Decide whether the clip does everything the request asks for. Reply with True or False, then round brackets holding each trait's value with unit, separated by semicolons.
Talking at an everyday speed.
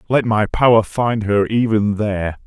True (170 wpm)